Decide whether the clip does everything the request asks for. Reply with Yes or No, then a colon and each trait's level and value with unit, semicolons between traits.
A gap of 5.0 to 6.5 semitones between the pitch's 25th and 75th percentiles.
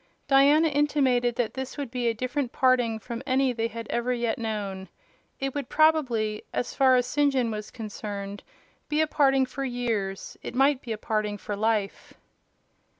No: average, 3.6 semitones